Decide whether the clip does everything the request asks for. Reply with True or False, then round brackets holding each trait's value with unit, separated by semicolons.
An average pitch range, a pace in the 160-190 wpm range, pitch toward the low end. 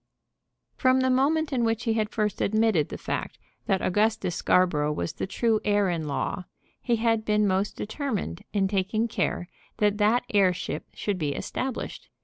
False (3.5 semitones; 165 wpm; 210 Hz)